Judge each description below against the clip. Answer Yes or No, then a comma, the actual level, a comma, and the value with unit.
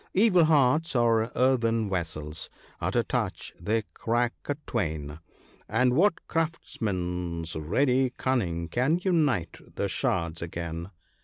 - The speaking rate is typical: No, slow, 125 wpm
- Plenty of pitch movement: Yes, wide, 7.8 semitones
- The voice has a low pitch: Yes, low, 115 Hz